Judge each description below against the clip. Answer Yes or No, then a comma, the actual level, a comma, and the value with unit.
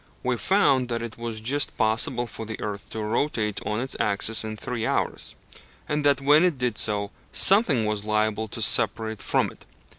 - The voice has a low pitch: Yes, low, 115 Hz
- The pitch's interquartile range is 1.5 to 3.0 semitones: No, average, 3.6 semitones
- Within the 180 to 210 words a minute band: Yes, average, 185 wpm